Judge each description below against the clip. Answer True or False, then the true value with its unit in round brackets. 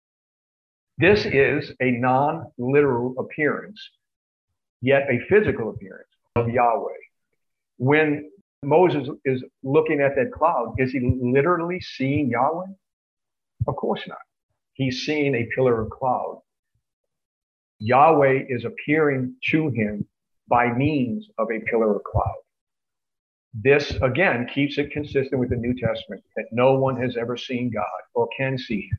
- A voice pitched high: False (135 Hz)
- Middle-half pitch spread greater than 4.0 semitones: False (3.4 semitones)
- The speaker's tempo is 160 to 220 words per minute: False (135 wpm)